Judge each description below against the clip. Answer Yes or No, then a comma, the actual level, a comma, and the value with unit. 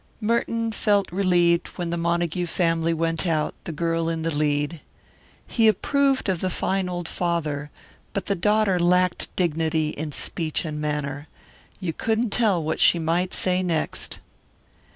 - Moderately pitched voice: Yes, medium, 170 Hz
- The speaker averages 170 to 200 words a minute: No, average, 150 wpm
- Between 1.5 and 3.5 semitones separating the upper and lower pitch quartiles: Yes, average, 2.7 semitones